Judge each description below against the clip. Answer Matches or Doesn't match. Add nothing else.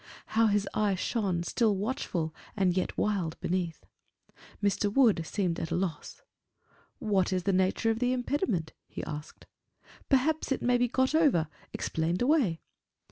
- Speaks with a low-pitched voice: Doesn't match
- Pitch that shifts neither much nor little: Doesn't match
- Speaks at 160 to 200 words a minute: Doesn't match